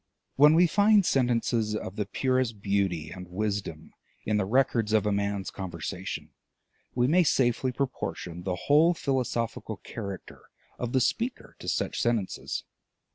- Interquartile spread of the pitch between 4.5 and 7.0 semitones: Yes, average, 5.0 semitones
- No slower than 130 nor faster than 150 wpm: Yes, average, 140 wpm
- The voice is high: No, low, 110 Hz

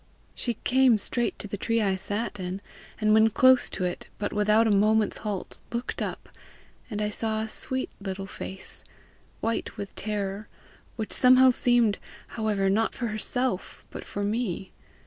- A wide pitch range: No, narrow, 2.6 semitones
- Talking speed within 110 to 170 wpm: Yes, average, 165 wpm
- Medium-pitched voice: No, high, 215 Hz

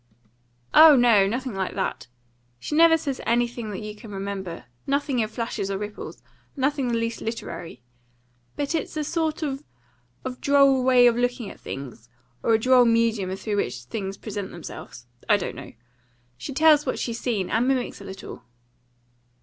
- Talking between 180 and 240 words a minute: No, average, 165 wpm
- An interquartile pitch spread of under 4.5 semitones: No, average, 5.2 semitones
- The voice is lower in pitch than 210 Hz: No, high, 230 Hz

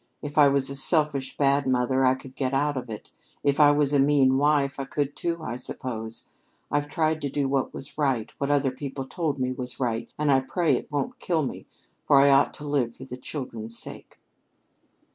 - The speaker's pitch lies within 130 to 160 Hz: Yes, medium, 140 Hz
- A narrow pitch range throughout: Yes, narrow, 2.0 semitones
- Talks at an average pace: No, fast, 215 wpm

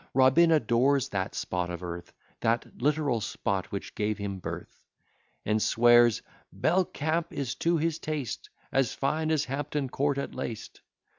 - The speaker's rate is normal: Yes, average, 145 wpm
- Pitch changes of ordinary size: No, wide, 5.9 semitones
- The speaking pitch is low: Yes, low, 130 Hz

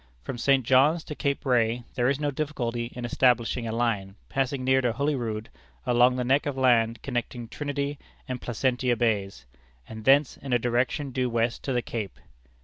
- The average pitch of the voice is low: Yes, low, 125 Hz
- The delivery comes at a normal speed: Yes, average, 180 wpm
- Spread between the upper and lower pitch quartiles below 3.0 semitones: Yes, narrow, 2.5 semitones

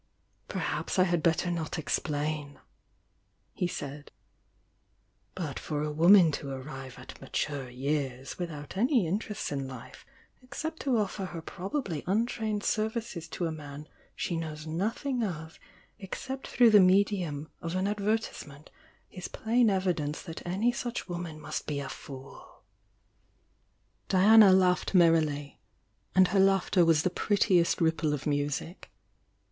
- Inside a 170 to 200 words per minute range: No, average, 145 wpm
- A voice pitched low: No, medium, 170 Hz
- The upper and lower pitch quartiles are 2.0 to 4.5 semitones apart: No, average, 5.1 semitones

